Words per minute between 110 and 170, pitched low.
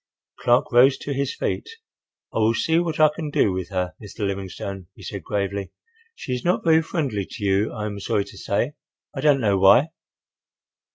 No: average, 185 wpm; low, 110 Hz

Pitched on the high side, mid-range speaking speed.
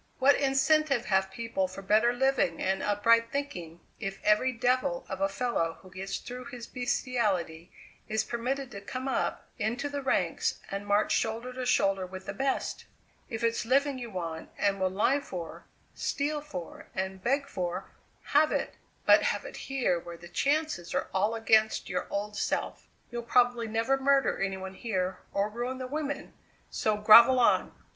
Yes: high, 230 Hz; average, 170 wpm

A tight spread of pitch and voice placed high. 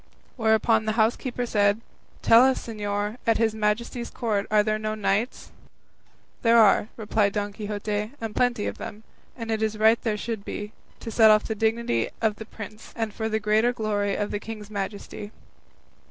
Yes: narrow, 1.4 semitones; high, 215 Hz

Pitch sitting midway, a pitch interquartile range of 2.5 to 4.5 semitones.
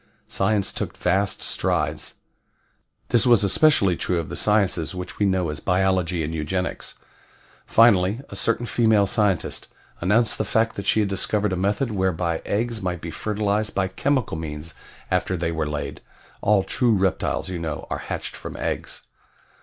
No: very low, 95 Hz; average, 3.3 semitones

